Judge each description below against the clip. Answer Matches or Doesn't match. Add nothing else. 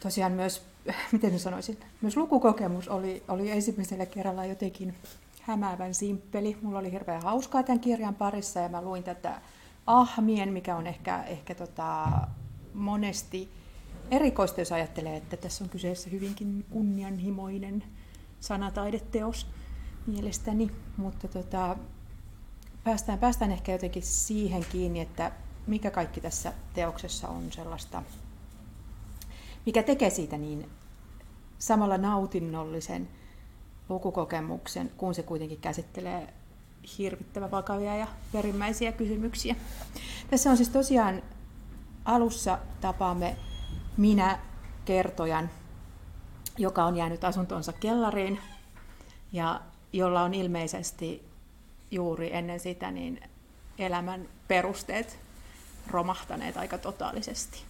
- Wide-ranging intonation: Doesn't match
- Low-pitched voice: Doesn't match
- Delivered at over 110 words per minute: Doesn't match